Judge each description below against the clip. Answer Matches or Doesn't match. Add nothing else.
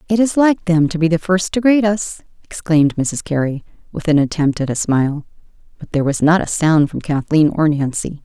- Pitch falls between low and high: Matches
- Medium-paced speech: Doesn't match